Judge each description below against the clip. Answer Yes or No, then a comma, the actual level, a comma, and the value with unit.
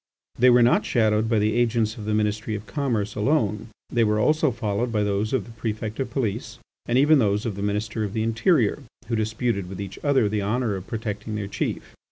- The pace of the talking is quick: Yes, fast, 225 wpm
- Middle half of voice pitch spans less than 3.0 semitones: Yes, narrow, 2.4 semitones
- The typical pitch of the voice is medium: No, low, 110 Hz